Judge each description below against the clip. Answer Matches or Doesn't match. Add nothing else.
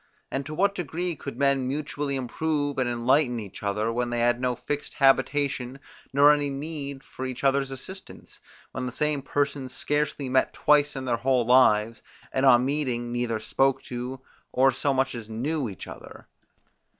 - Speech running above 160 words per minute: Matches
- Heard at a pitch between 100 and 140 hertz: Matches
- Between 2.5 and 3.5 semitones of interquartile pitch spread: Matches